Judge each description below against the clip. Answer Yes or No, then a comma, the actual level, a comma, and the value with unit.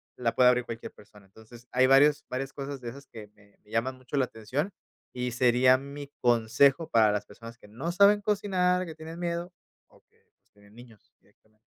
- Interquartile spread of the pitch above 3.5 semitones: Yes, average, 4.3 semitones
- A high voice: No, low, 125 Hz